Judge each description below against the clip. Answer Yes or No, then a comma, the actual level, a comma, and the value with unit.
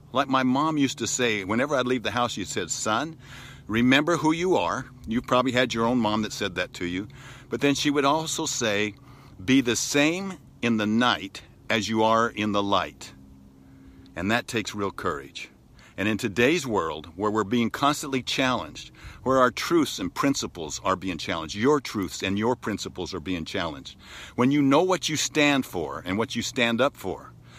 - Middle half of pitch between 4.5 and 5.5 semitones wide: Yes, average, 5.0 semitones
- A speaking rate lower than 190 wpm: No, average, 195 wpm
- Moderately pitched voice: No, low, 115 Hz